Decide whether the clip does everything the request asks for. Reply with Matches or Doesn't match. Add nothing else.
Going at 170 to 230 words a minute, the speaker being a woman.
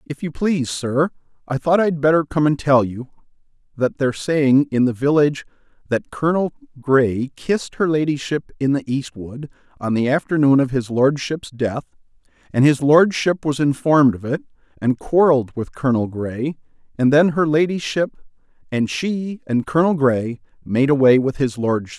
Doesn't match